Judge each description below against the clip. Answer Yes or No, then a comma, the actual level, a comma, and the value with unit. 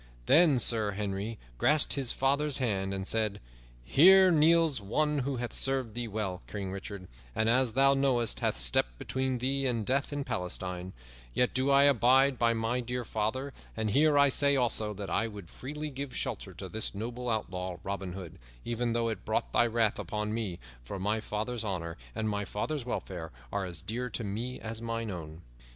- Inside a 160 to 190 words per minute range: Yes, average, 185 wpm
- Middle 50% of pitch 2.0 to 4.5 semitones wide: No, average, 4.9 semitones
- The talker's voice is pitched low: Yes, low, 115 Hz